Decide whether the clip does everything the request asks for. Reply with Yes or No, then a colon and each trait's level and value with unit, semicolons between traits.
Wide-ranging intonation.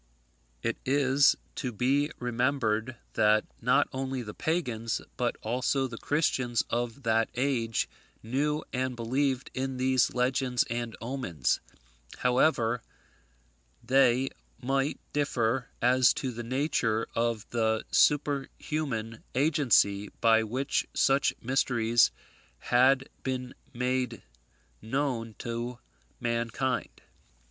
No: average, 2.7 semitones